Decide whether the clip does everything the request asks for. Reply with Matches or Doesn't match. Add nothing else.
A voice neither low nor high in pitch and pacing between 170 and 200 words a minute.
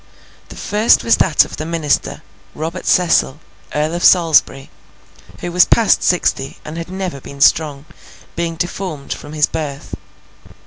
Doesn't match